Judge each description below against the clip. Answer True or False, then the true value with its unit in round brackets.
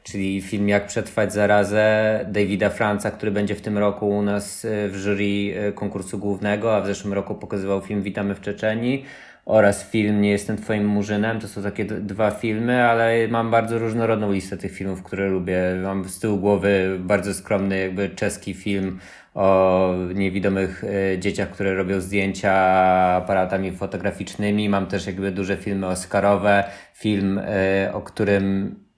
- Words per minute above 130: True (155 wpm)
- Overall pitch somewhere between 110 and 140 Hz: False (100 Hz)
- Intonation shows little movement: True (1.4 semitones)